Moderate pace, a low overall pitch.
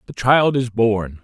Yes: average, 195 wpm; low, 115 Hz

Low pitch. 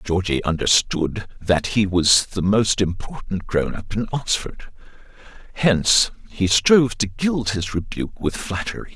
Yes: low, 105 Hz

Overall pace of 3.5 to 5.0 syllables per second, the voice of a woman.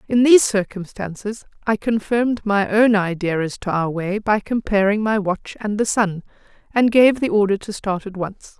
Yes: 4.8 syllables/s; female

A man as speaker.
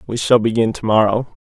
Yes: male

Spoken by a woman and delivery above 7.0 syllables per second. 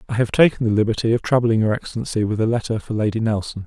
No: male; 7.2 syllables/s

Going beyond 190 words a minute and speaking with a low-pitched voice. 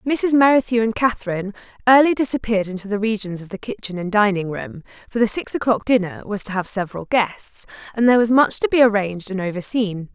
No: average, 200 wpm; high, 215 Hz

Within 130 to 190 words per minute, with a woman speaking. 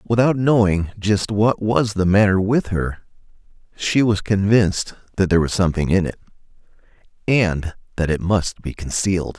No: average, 155 wpm; male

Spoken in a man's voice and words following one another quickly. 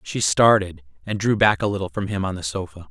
Yes: male; fast, 250 wpm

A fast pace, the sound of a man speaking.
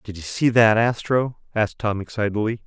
No: average, 180 wpm; male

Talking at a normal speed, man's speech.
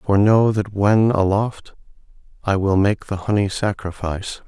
Yes: average, 145 wpm; male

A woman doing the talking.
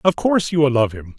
No: male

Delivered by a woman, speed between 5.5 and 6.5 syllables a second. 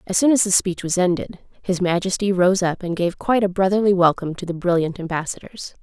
Yes: female; 6.0 syllables/s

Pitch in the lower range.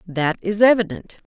No: high, 195 Hz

